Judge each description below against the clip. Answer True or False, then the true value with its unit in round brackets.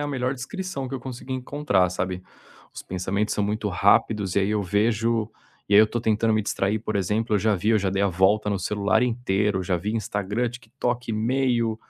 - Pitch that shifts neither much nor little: True (3.1 semitones)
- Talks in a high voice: False (110 Hz)